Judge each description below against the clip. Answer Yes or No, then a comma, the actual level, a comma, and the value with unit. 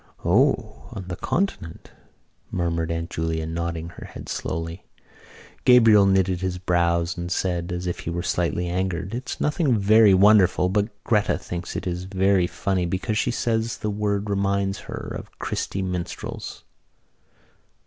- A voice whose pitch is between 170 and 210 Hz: No, very low, 95 Hz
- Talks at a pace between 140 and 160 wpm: Yes, average, 145 wpm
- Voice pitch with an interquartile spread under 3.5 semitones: Yes, average, 3.0 semitones